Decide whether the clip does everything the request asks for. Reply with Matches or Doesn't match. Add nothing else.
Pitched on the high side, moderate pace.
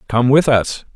Doesn't match